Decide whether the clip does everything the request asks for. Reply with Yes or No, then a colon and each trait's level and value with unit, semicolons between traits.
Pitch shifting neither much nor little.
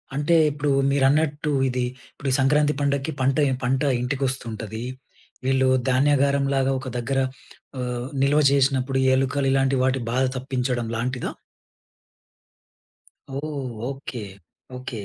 No: narrow, 1.7 semitones